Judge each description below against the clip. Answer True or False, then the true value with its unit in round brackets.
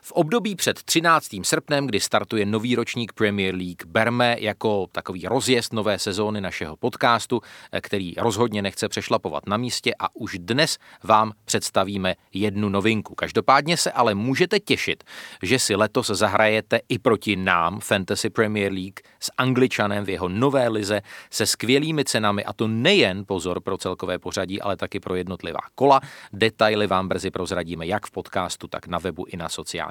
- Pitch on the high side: False (105 Hz)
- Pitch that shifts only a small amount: False (3.9 semitones)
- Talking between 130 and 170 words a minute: True (165 wpm)